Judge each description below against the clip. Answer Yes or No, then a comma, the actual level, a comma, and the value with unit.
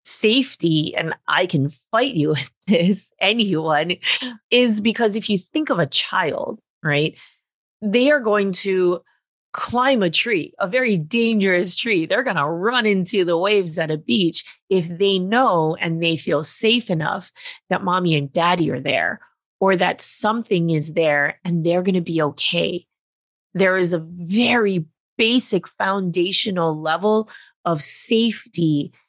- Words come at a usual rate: Yes, average, 150 wpm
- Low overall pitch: No, medium, 185 Hz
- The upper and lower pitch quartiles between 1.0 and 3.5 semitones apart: No, average, 4.7 semitones